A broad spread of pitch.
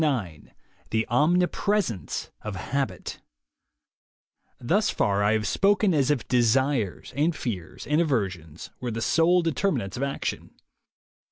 Yes: wide, 7.4 semitones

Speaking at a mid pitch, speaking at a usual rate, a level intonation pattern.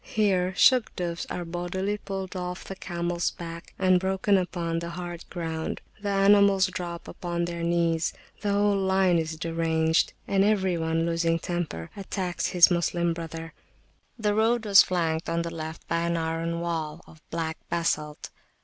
Yes: medium, 175 Hz; average, 160 wpm; narrow, 2.3 semitones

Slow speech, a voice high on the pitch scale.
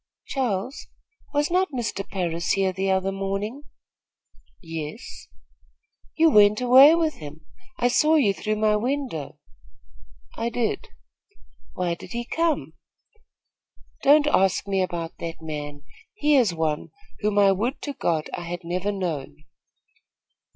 Yes: slow, 130 wpm; high, 200 Hz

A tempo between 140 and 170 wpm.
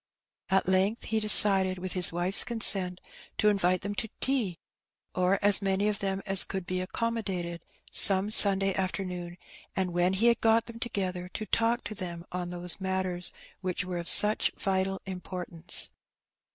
Yes: average, 165 wpm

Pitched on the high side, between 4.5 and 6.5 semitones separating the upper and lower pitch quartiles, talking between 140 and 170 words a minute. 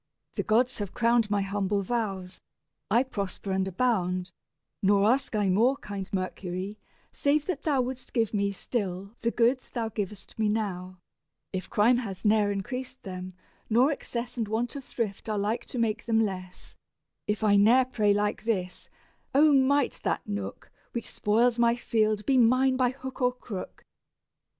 No: high, 215 Hz; average, 3.8 semitones; average, 165 wpm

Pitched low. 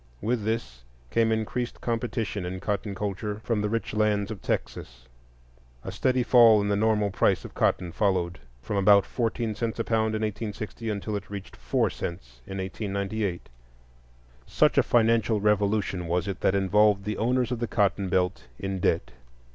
Yes: low, 105 Hz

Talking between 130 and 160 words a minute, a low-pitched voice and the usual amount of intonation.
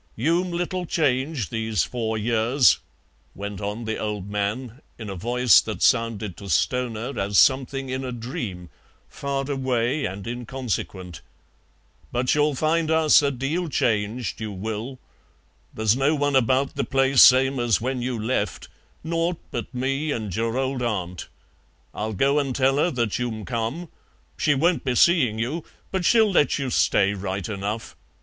Yes: average, 155 wpm; low, 125 Hz; average, 4.2 semitones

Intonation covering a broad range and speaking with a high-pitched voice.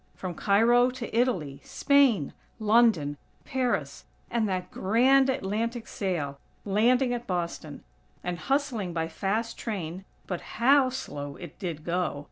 Yes: wide, 5.9 semitones; high, 210 Hz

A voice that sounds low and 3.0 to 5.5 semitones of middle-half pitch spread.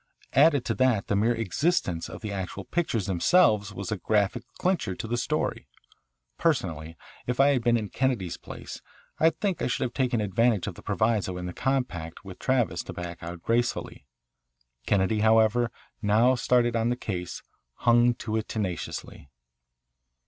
Yes: low, 110 Hz; average, 4.5 semitones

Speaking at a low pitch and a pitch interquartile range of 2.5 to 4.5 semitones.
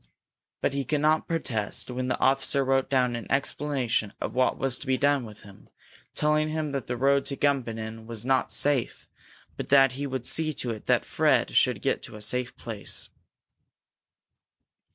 Yes: low, 130 Hz; average, 3.0 semitones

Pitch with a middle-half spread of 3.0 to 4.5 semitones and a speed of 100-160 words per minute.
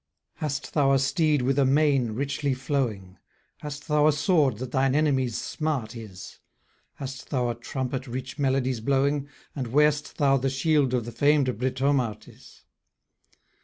No: narrow, 2.4 semitones; average, 150 wpm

